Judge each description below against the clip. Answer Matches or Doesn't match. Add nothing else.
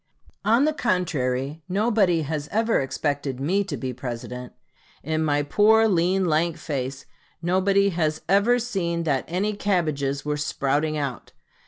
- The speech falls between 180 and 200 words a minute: Doesn't match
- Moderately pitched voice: Matches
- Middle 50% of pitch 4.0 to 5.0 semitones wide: Doesn't match